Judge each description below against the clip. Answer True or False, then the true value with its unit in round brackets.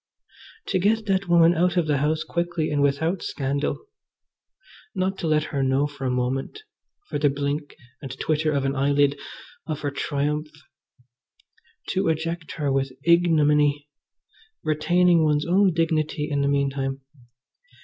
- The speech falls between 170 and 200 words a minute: False (145 wpm)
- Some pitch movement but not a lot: True (3.1 semitones)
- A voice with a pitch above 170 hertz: False (150 Hz)